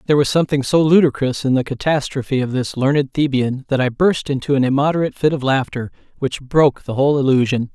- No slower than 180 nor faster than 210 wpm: Yes, average, 200 wpm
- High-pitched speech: No, low, 135 Hz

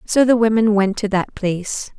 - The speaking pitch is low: No, high, 210 Hz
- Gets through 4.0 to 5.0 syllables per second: Yes, 4.9 syllables/s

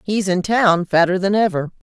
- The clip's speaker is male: No, female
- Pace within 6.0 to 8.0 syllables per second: No, 4.9 syllables/s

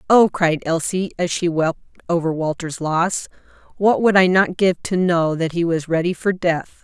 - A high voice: No, medium, 170 Hz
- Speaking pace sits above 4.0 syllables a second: Yes, 4.6 syllables/s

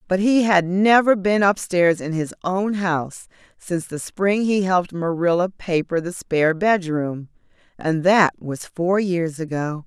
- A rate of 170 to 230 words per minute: No, average, 160 wpm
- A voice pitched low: No, medium, 180 Hz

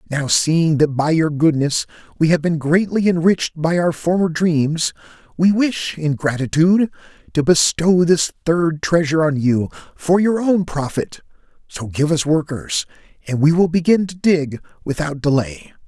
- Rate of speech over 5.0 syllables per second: No, 4.5 syllables/s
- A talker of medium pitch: Yes, medium, 160 Hz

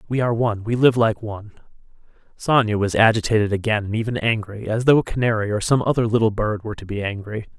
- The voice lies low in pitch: Yes, low, 110 Hz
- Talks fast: Yes, fast, 215 wpm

